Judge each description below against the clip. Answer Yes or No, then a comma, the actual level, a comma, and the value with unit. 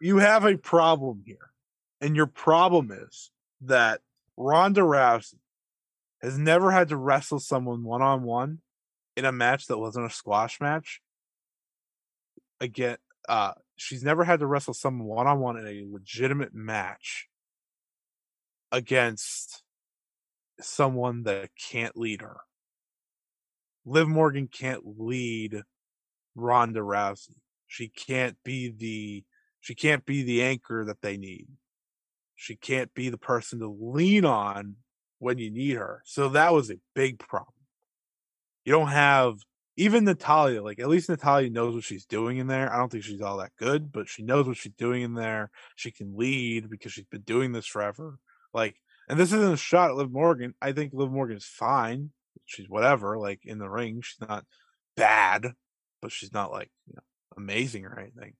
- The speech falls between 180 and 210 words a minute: No, average, 160 wpm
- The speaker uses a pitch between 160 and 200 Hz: No, low, 125 Hz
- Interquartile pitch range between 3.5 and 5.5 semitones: Yes, average, 4.2 semitones